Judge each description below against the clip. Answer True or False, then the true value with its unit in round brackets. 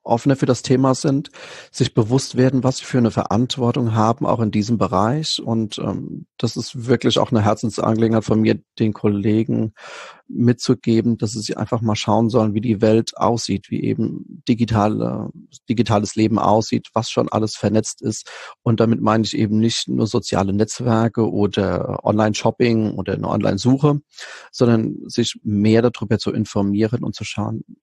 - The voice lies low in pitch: True (110 Hz)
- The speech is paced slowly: False (165 wpm)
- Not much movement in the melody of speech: True (2.1 semitones)